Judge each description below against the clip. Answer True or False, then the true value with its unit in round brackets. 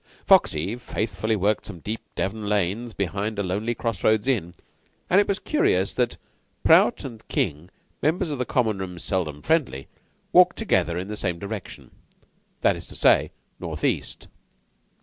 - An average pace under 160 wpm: True (150 wpm)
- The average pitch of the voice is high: False (105 Hz)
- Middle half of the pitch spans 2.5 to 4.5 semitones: False (4.9 semitones)